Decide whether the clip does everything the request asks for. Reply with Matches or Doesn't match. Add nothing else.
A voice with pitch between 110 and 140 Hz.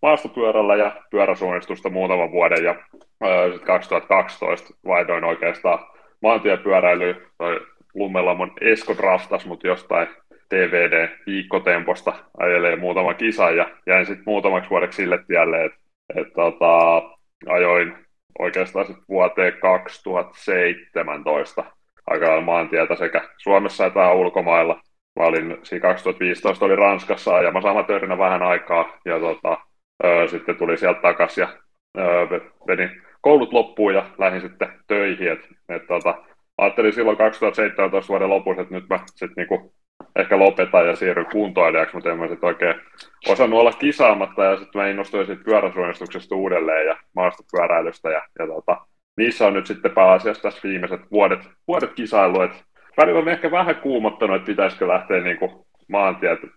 Doesn't match